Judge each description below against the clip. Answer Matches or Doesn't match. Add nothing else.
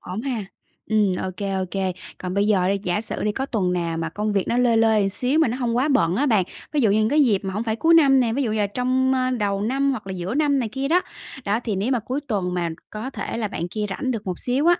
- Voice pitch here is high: Matches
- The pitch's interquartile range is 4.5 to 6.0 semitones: Matches